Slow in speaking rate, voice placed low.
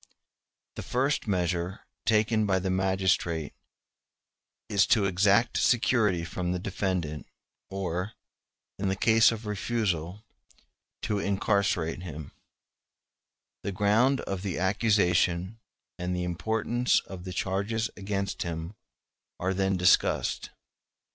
Yes: slow, 110 wpm; very low, 95 Hz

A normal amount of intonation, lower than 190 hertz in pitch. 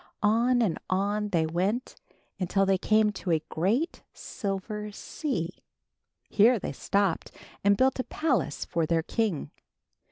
No: average, 3.8 semitones; high, 200 Hz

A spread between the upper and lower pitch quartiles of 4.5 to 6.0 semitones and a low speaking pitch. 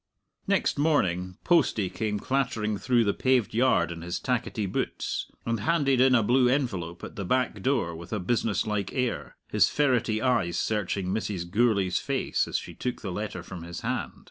Yes: wide, 5.4 semitones; low, 110 Hz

